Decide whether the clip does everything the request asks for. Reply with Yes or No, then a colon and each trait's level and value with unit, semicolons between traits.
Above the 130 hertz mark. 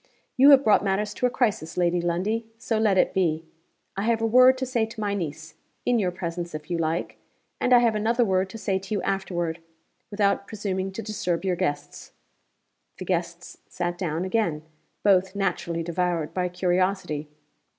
Yes: high, 190 Hz